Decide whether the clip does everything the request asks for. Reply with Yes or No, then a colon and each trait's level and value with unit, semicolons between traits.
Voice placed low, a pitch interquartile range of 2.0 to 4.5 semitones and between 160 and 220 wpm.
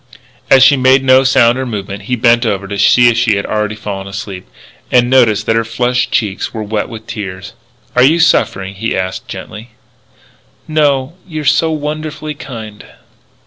Yes: low, 115 Hz; average, 4.2 semitones; average, 180 wpm